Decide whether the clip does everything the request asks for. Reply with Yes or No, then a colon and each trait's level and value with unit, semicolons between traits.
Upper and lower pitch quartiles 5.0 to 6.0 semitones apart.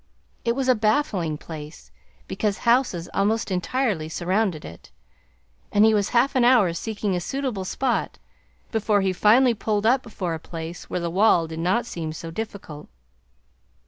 Yes: wide, 5.5 semitones